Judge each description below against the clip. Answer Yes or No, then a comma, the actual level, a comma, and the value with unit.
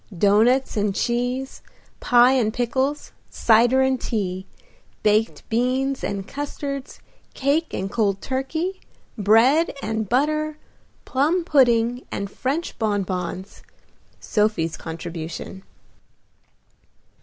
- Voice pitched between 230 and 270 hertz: Yes, high, 240 Hz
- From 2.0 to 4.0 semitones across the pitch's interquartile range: No, average, 4.7 semitones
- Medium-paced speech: No, slow, 95 wpm